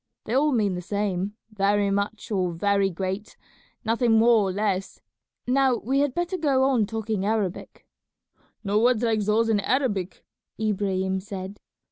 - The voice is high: Yes, high, 210 Hz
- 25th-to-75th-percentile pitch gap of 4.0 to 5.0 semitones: No, average, 3.0 semitones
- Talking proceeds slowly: No, average, 150 wpm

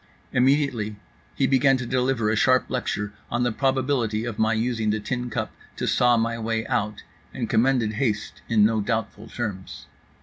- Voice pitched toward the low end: Yes, low, 115 Hz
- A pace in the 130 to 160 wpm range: No, average, 170 wpm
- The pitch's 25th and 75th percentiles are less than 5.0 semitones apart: Yes, average, 3.1 semitones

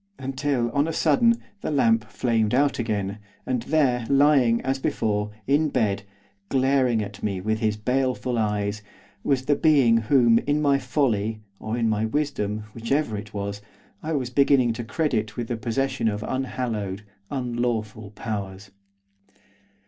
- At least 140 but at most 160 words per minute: Yes, average, 150 wpm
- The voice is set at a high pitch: No, low, 120 Hz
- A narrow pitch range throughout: No, average, 4.2 semitones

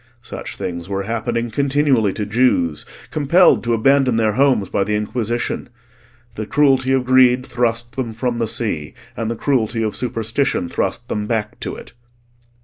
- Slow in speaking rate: No, average, 160 wpm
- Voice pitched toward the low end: Yes, low, 115 Hz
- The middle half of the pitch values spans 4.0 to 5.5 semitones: No, average, 3.2 semitones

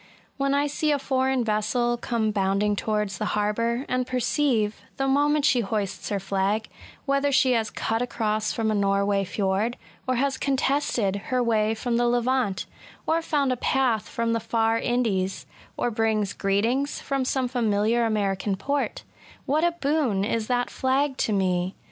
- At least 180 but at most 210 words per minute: No, average, 165 wpm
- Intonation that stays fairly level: No, average, 4.0 semitones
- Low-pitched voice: No, high, 230 Hz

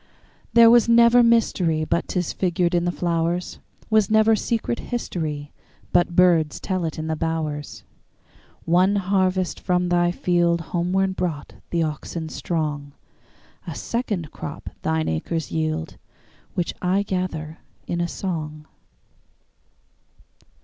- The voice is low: No, medium, 175 Hz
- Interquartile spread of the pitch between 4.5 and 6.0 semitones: No, average, 2.9 semitones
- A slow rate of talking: Yes, slow, 105 wpm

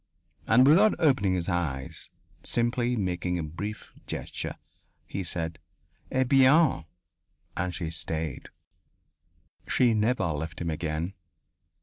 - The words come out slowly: Yes, slow, 110 wpm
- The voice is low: Yes, very low, 95 Hz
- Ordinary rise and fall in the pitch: No, wide, 7.1 semitones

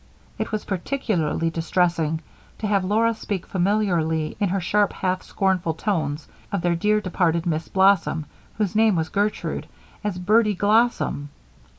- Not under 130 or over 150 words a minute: Yes, average, 145 wpm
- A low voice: No, medium, 185 Hz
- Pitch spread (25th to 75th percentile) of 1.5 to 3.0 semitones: No, average, 4.0 semitones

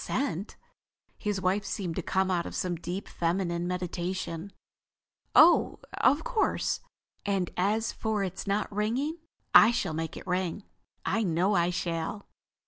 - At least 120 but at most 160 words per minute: Yes, slow, 135 wpm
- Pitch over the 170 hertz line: Yes, high, 190 Hz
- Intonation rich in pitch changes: No, average, 3.2 semitones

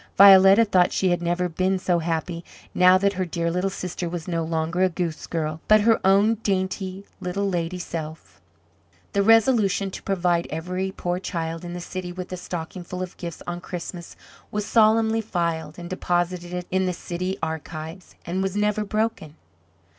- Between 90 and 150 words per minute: No, average, 175 wpm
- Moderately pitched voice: Yes, medium, 180 Hz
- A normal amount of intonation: No, narrow, 2.2 semitones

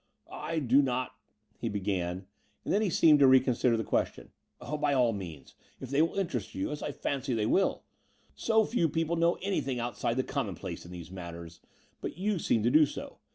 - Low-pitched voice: Yes, low, 130 Hz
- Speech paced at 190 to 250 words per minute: Yes, average, 200 wpm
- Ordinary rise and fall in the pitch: No, wide, 7.1 semitones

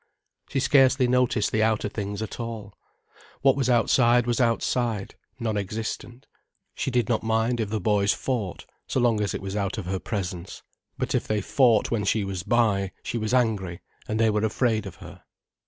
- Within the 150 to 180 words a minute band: No, average, 190 wpm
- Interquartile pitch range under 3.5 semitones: Yes, average, 2.8 semitones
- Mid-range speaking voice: No, low, 110 Hz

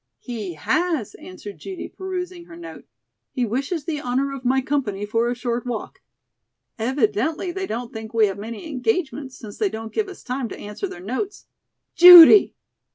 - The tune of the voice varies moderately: No, wide, 7.5 semitones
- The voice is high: Yes, very high, 255 Hz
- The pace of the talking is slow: No, average, 170 wpm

